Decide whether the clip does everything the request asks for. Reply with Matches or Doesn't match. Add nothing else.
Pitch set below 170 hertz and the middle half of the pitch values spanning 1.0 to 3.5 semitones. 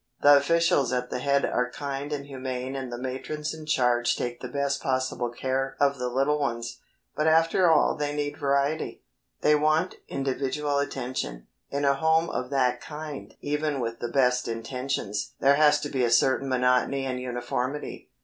Matches